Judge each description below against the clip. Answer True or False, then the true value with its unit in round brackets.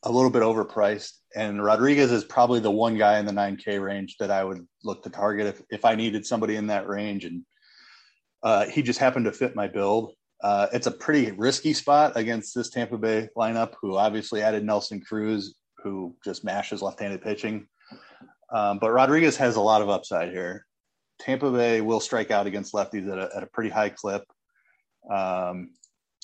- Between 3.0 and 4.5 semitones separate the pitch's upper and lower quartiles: False (2.6 semitones)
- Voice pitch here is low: True (110 Hz)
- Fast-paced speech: False (190 wpm)